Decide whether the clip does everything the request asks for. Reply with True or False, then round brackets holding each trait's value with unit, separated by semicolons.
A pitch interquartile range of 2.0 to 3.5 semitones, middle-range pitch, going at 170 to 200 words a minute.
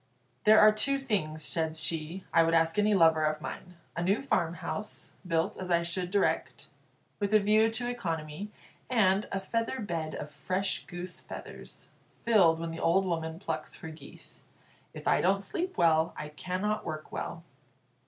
False (4.3 semitones; 180 Hz; 175 wpm)